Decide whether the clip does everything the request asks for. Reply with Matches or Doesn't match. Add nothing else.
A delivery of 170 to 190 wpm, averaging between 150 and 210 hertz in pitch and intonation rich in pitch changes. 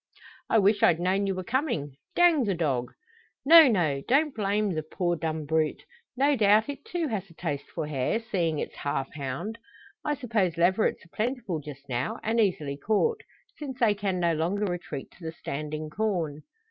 Matches